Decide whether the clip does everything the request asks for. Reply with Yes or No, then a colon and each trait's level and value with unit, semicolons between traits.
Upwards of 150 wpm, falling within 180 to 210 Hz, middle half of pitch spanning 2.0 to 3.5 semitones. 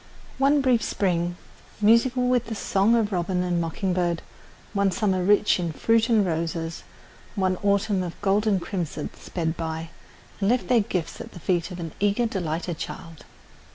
No: average, 170 wpm; high, 190 Hz; average, 4.1 semitones